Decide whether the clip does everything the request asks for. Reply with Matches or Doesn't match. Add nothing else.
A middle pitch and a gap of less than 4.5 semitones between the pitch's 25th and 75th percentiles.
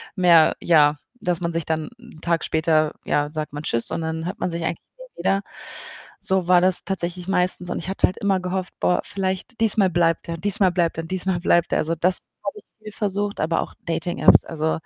Matches